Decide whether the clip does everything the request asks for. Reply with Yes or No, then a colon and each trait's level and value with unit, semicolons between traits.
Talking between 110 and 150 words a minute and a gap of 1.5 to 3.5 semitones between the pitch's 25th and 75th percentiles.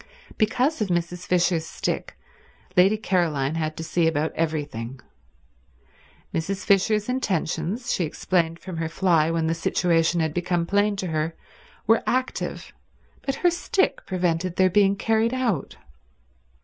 No: slow, 135 wpm; average, 3.9 semitones